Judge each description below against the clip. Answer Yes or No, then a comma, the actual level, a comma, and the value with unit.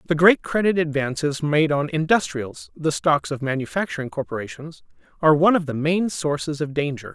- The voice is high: No, medium, 150 Hz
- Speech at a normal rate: Yes, average, 170 wpm